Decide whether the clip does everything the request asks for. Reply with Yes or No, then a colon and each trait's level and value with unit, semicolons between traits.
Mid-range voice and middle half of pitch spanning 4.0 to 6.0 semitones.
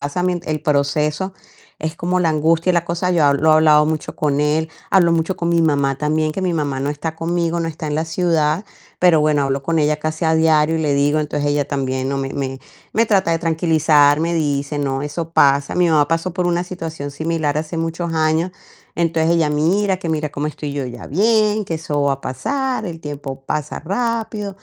No: medium, 155 Hz; average, 2.7 semitones